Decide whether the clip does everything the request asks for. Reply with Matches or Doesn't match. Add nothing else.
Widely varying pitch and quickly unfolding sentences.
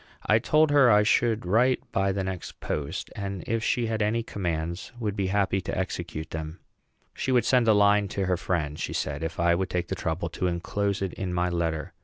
Doesn't match